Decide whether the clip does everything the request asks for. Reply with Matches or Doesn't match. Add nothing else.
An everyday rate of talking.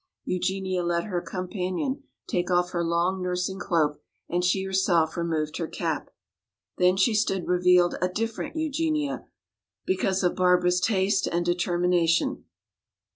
Doesn't match